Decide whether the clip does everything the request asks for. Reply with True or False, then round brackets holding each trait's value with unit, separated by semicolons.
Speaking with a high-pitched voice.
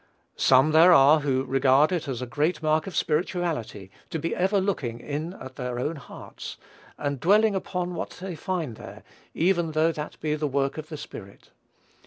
False (155 Hz)